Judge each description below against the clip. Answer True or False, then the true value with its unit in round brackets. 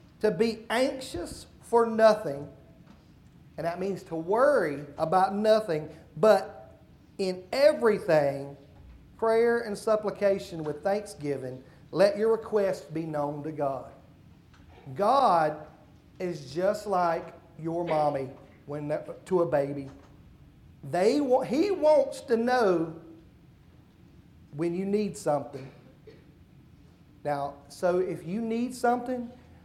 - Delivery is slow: True (105 wpm)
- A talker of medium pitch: True (180 Hz)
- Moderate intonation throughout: False (6.6 semitones)